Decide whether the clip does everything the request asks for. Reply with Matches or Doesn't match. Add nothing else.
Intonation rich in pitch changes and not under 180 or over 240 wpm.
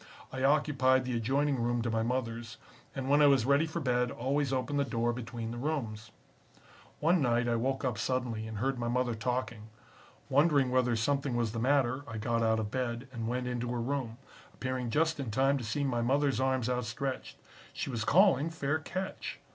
Doesn't match